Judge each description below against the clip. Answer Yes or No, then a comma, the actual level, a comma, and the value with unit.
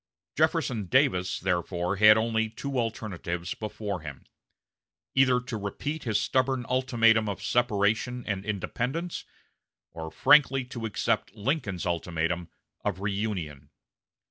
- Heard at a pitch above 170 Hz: No, low, 110 Hz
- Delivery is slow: Yes, slow, 115 wpm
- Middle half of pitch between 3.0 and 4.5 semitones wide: No, average, 5.1 semitones